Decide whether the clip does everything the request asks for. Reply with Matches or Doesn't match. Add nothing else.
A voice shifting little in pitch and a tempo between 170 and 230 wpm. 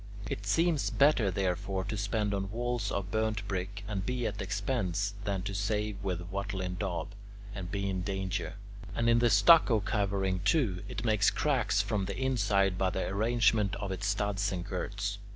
Matches